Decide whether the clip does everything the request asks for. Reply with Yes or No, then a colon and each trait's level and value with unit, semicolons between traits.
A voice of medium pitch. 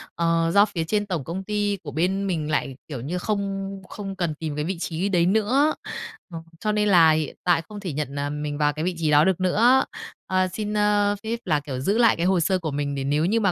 Yes: medium, 180 Hz